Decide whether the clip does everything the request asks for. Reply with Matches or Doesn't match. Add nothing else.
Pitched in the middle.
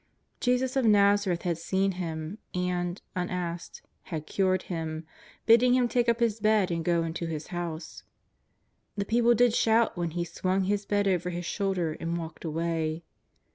Matches